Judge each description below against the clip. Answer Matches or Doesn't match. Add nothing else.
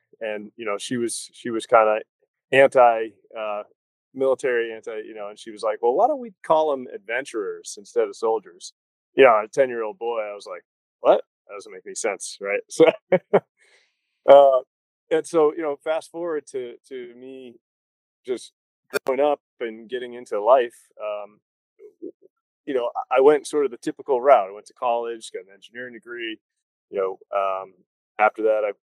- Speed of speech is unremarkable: Matches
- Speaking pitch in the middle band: Matches